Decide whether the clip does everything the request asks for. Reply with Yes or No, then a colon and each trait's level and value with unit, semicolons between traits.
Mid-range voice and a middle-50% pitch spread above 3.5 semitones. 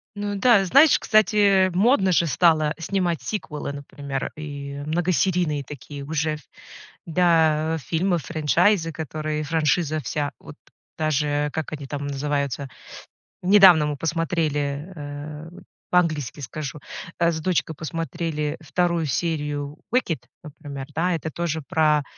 No: medium, 155 Hz; average, 2.8 semitones